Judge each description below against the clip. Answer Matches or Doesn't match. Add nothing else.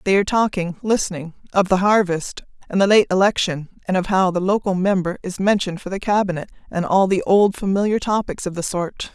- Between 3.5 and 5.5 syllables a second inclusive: Doesn't match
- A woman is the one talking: Matches